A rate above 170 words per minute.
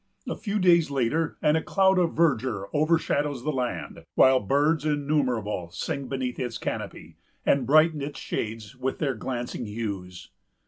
No: average, 150 wpm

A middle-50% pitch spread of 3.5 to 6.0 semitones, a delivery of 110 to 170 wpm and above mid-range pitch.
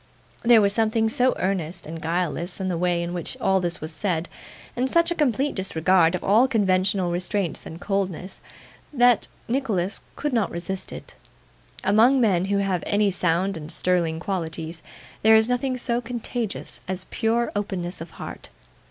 Yes: average, 4.5 semitones; average, 165 wpm; high, 195 Hz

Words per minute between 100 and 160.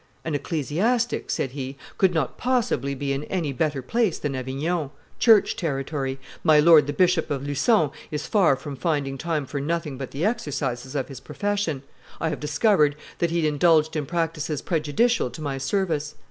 No: average, 175 wpm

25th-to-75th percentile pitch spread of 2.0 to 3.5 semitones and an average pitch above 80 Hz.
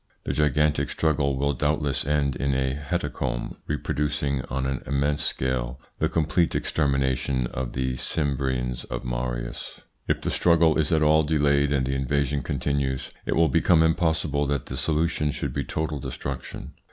No: narrow, 2.4 semitones; very low, 70 Hz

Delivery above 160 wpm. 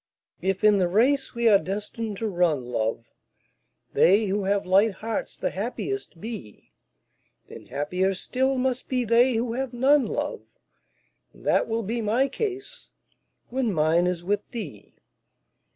No: average, 150 wpm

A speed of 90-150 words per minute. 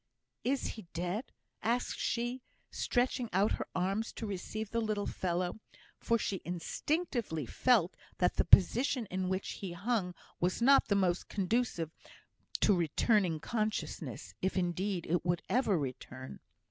Yes: average, 140 wpm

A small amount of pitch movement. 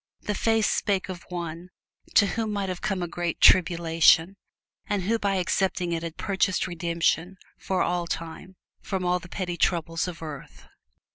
Yes: narrow, 2.3 semitones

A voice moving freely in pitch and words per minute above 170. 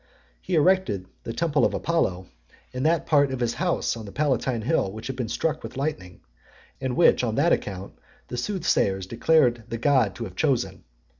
Yes: wide, 6.2 semitones; average, 190 wpm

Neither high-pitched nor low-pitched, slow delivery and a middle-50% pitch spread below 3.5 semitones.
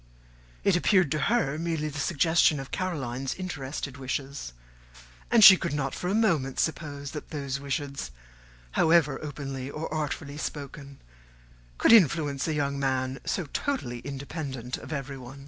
No: medium, 145 Hz; average, 145 wpm; average, 3.1 semitones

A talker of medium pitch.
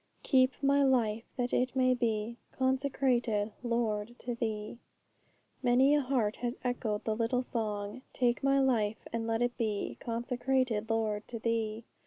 No: high, 235 Hz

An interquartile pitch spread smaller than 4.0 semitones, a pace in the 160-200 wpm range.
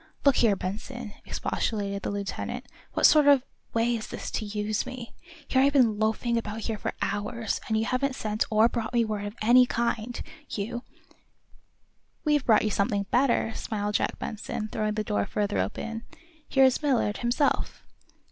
Yes: average, 2.8 semitones; average, 175 wpm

